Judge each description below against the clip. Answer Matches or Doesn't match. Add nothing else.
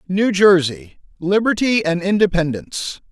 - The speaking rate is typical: Doesn't match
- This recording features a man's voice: Matches